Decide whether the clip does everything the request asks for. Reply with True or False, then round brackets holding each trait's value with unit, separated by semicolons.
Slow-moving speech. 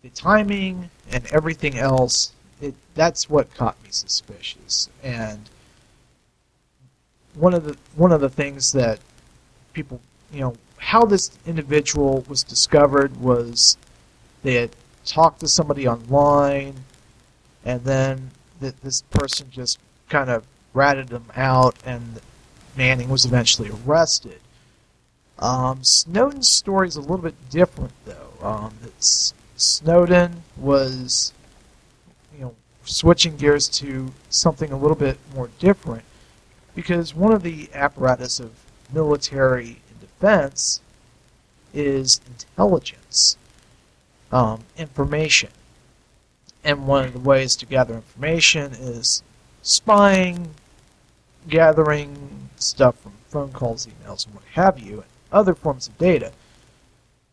True (120 wpm)